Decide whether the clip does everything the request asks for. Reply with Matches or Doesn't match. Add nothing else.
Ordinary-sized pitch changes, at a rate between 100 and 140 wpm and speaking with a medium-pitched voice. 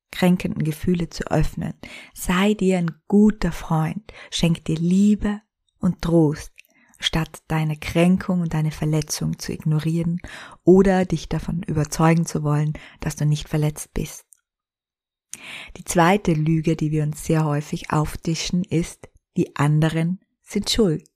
Matches